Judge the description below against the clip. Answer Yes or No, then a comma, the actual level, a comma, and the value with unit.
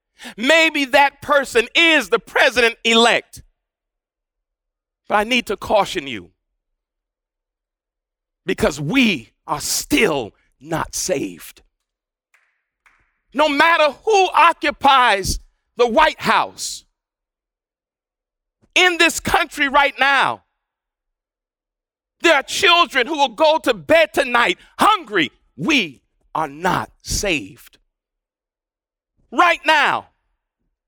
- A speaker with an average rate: No, slow, 90 wpm